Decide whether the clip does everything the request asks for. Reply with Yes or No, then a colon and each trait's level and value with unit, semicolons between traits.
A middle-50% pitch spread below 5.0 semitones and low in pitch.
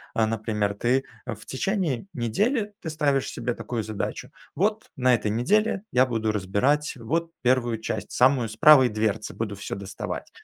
No: wide, 5.4 semitones; low, 125 Hz